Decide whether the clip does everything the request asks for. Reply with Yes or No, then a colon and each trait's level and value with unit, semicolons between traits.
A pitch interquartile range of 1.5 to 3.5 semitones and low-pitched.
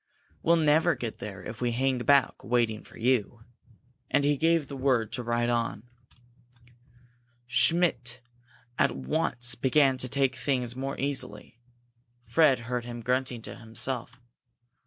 Yes: average, 2.7 semitones; low, 125 Hz